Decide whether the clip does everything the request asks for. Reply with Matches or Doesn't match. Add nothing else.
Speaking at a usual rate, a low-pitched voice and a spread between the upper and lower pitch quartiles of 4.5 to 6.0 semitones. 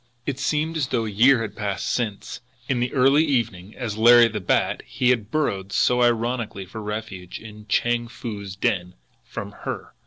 Doesn't match